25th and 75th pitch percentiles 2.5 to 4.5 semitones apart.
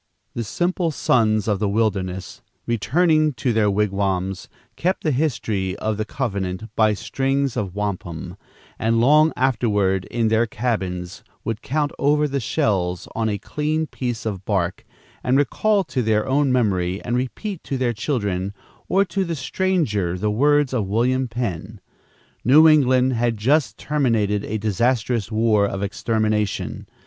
No: average, 5.0 semitones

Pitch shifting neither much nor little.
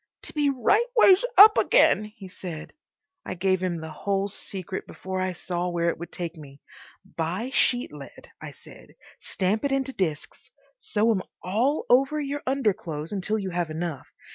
No: wide, 6.6 semitones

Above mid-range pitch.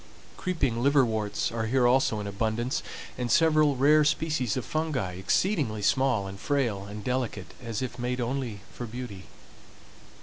No: low, 125 Hz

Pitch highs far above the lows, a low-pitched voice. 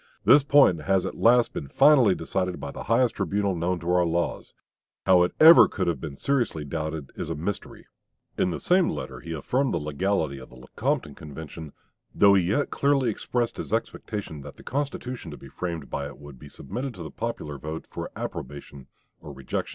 Yes: wide, 7.5 semitones; very low, 90 Hz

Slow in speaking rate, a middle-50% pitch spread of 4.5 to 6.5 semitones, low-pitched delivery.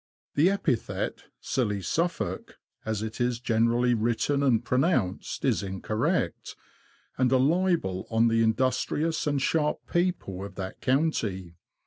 Yes: slow, 130 wpm; average, 5.1 semitones; low, 120 Hz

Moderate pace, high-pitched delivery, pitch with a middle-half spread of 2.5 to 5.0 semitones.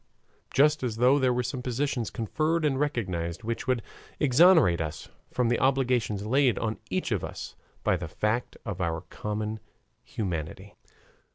No: average, 155 wpm; low, 120 Hz; average, 4.6 semitones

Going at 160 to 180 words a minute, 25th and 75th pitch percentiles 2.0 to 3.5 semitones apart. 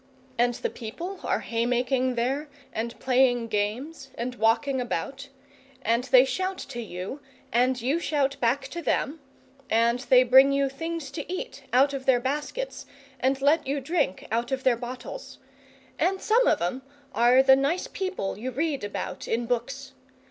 Yes: average, 165 wpm; average, 2.9 semitones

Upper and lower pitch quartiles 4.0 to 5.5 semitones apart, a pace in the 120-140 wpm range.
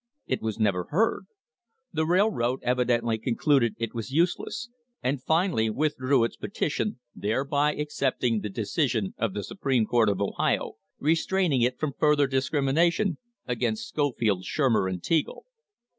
Yes: average, 5.1 semitones; slow, 135 wpm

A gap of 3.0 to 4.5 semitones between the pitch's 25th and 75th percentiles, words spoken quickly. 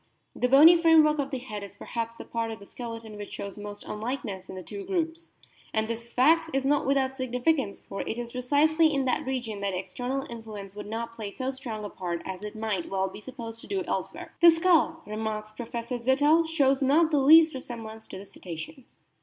No: average, 5.2 semitones; fast, 210 wpm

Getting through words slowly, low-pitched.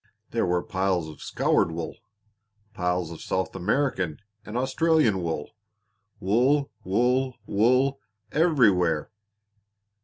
Yes: slow, 100 wpm; low, 105 Hz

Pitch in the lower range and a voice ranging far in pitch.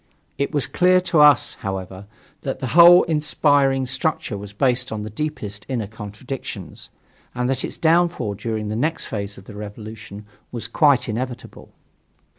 Yes: low, 125 Hz; wide, 5.9 semitones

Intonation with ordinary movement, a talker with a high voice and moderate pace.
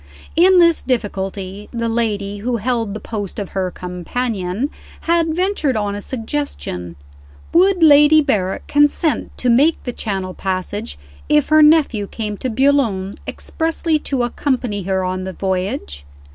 No: wide, 7.1 semitones; high, 230 Hz; average, 145 wpm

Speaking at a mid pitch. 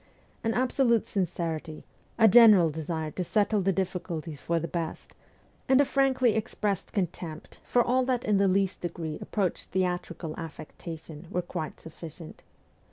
Yes: medium, 180 Hz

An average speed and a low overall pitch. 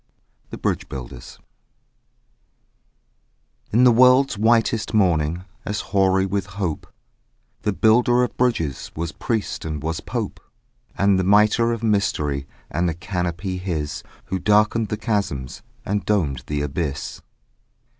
No: slow, 125 wpm; very low, 95 Hz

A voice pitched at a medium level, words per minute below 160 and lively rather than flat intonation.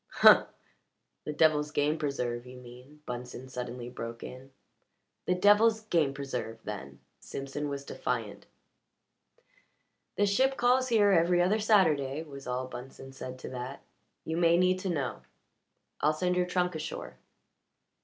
Yes: medium, 150 Hz; average, 140 wpm; wide, 5.9 semitones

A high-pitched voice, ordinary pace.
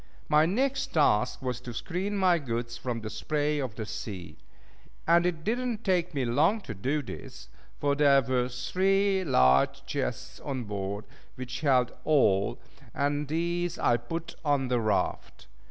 No: medium, 140 Hz; average, 160 wpm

